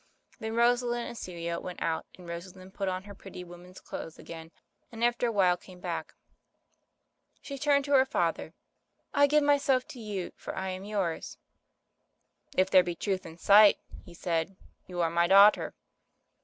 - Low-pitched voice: No, high, 190 Hz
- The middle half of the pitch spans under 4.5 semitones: No, average, 5.2 semitones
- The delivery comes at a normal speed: Yes, average, 175 wpm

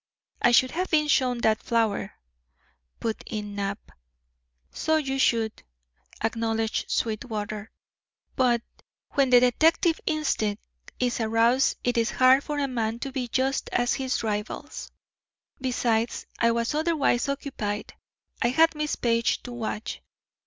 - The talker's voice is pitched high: Yes, high, 240 Hz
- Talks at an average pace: No, slow, 130 wpm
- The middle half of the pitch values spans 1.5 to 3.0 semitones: No, average, 3.4 semitones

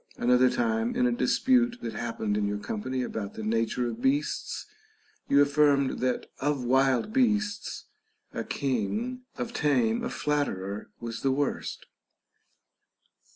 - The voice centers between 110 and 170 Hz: Yes, low, 135 Hz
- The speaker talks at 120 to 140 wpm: Yes, slow, 135 wpm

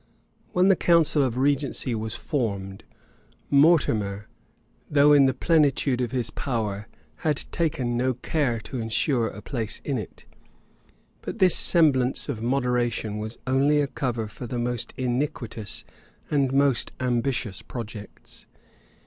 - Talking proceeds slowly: Yes, slow, 130 wpm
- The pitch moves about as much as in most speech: Yes, average, 3.8 semitones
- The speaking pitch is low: Yes, low, 125 Hz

